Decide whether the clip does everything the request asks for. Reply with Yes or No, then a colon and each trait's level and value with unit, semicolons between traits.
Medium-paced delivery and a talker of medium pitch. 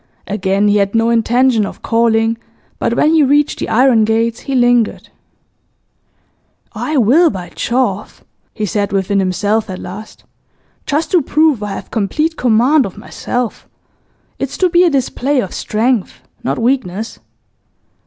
No: average, 145 wpm; high, 230 Hz